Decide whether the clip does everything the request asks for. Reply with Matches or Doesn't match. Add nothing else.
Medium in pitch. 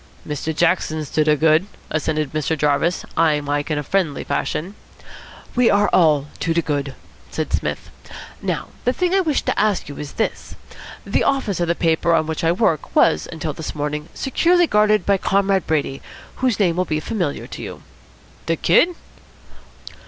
Matches